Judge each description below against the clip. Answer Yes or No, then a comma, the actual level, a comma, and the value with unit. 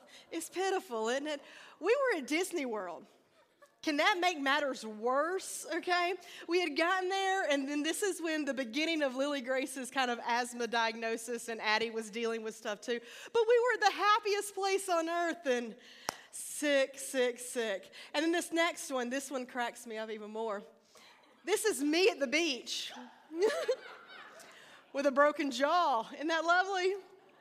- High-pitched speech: Yes, very high, 290 Hz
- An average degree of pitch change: No, wide, 6.6 semitones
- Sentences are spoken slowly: No, average, 170 wpm